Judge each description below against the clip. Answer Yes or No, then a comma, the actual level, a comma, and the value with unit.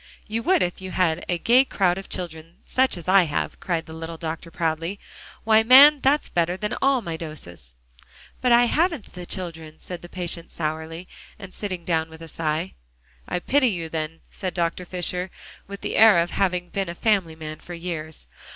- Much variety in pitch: No, average, 3.5 semitones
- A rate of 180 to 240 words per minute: Yes, average, 195 wpm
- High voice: No, medium, 175 Hz